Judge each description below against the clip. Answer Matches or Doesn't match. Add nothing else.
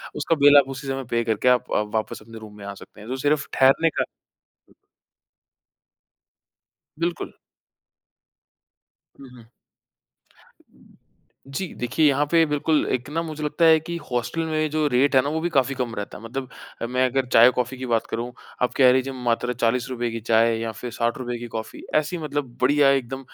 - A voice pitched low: Matches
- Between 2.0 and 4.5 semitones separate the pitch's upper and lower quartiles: Matches